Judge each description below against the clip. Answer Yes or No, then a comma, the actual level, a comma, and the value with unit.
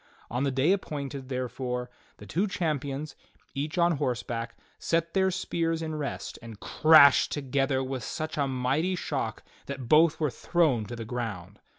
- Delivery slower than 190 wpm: Yes, average, 160 wpm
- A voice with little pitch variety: No, average, 4.2 semitones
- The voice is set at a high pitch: No, medium, 140 Hz